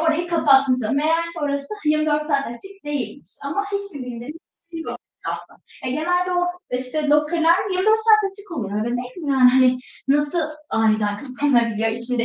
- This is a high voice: Yes, very high, 290 Hz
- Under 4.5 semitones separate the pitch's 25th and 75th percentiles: No, average, 5.1 semitones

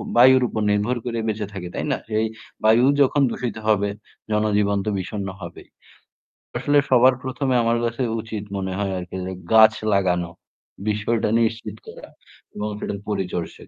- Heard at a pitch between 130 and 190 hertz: No, low, 105 Hz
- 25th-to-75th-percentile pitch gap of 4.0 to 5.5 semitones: No, average, 2.9 semitones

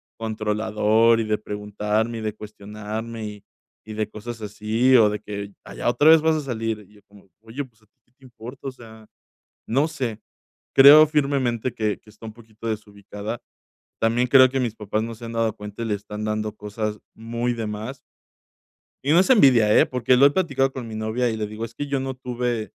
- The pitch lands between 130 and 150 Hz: No, low, 115 Hz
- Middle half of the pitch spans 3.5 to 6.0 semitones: No, average, 2.9 semitones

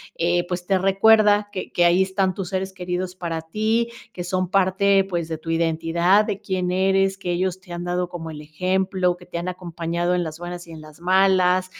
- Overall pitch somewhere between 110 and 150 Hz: No, medium, 180 Hz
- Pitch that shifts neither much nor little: No, narrow, 1.7 semitones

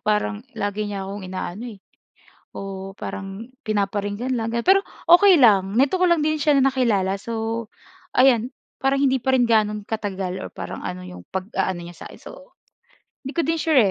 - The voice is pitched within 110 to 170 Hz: No, high, 215 Hz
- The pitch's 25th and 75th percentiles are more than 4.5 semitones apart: Yes, average, 5.2 semitones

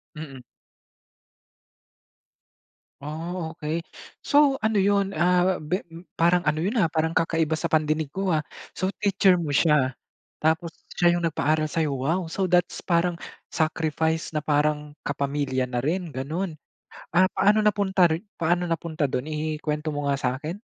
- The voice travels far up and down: No, average, 2.9 semitones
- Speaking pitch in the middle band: Yes, medium, 160 Hz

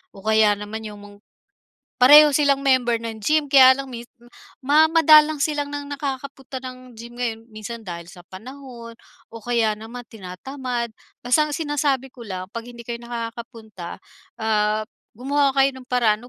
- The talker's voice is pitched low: No, high, 245 Hz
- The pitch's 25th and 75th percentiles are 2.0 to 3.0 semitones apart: No, average, 3.9 semitones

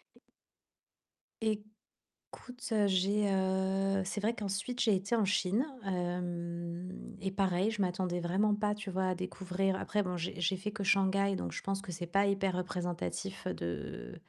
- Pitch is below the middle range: No, high, 190 Hz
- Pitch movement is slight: Yes, narrow, 2.1 semitones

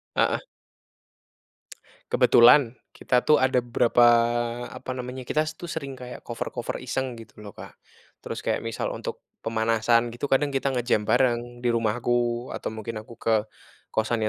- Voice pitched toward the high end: No, low, 120 Hz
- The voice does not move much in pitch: Yes, narrow, 2.0 semitones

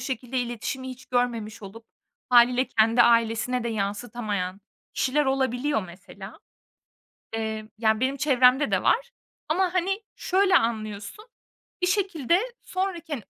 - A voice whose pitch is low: No, high, 245 Hz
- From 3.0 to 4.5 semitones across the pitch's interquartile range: No, average, 5.1 semitones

